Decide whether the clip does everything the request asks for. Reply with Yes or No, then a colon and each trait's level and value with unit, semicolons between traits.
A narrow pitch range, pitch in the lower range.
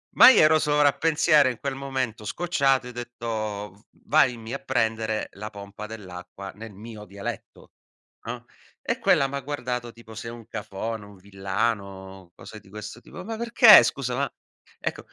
No: average, 4.7 semitones; low, 115 Hz